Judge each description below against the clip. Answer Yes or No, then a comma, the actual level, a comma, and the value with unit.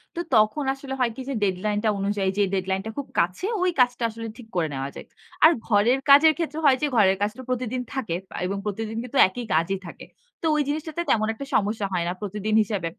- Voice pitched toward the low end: No, high, 220 Hz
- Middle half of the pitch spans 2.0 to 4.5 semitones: No, average, 5.3 semitones